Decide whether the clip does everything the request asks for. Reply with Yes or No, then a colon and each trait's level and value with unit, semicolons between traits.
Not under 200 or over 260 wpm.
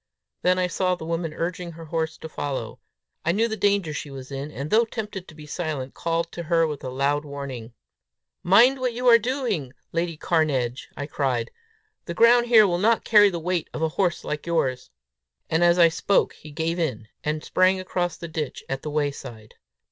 Yes: fast, 205 wpm